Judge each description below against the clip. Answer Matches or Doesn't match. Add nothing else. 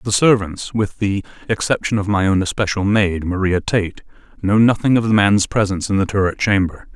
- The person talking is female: Doesn't match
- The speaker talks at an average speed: Matches